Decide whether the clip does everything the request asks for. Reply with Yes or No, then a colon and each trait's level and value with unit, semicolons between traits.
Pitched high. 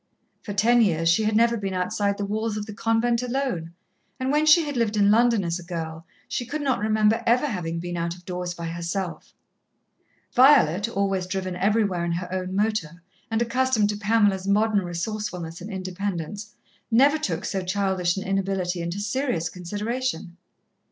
Yes: high, 200 Hz